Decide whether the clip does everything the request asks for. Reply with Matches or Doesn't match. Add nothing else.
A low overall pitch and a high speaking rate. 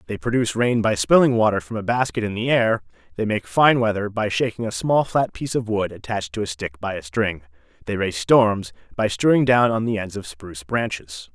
Matches